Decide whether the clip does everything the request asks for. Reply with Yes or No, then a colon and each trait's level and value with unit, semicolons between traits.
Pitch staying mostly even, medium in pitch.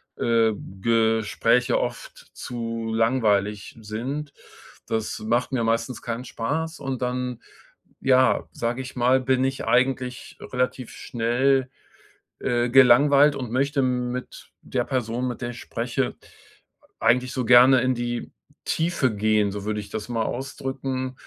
No: narrow, 2.3 semitones; low, 125 Hz